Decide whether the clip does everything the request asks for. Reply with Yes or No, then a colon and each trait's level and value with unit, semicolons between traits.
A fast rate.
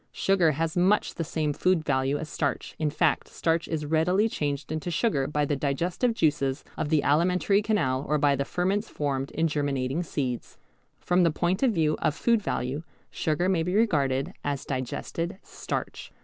No: average, 175 wpm